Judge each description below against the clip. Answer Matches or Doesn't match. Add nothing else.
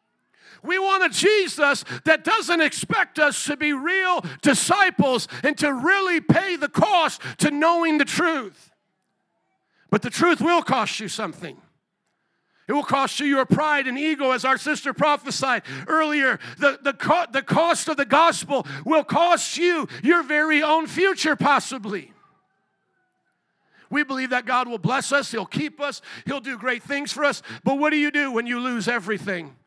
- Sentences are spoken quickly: Doesn't match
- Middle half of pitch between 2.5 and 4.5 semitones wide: Matches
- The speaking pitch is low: Doesn't match